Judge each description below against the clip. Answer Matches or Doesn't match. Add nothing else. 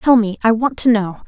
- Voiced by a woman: Matches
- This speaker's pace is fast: Matches